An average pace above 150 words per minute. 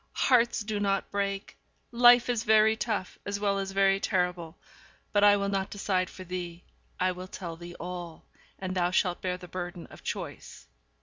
Yes: average, 180 wpm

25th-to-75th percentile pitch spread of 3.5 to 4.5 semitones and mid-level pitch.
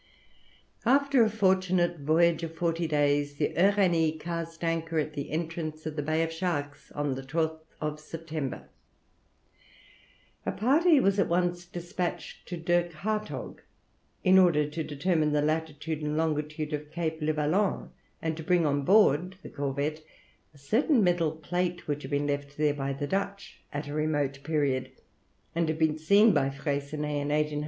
No: average, 2.9 semitones; medium, 160 Hz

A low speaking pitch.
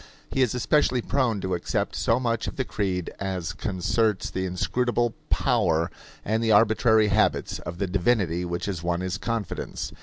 Yes: low, 105 Hz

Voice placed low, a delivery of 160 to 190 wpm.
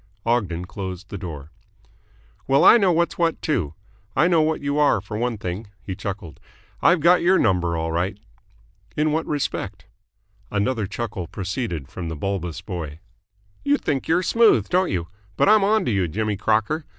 Yes: low, 105 Hz; average, 170 wpm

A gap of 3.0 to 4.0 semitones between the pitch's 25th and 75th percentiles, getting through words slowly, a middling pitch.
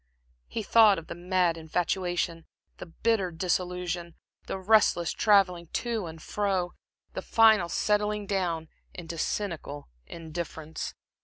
Yes: average, 3.4 semitones; slow, 115 wpm; medium, 180 Hz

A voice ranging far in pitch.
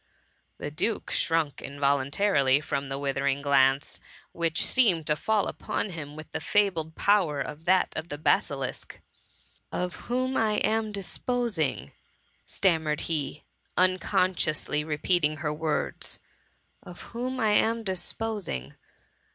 Yes: wide, 5.8 semitones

